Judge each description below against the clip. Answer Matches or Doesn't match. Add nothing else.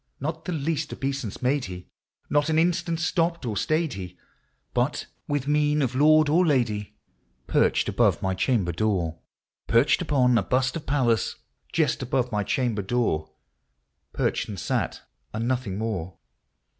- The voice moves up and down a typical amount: Doesn't match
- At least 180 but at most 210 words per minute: Doesn't match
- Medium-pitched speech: Doesn't match